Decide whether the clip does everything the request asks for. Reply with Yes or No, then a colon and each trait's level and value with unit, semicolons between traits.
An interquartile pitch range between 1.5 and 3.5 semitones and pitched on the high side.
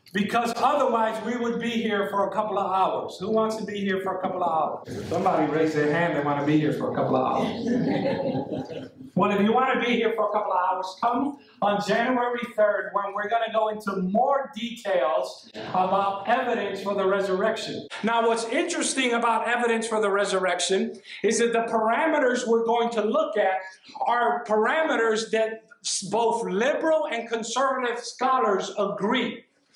Yes: average, 3.0 semitones; high, 220 Hz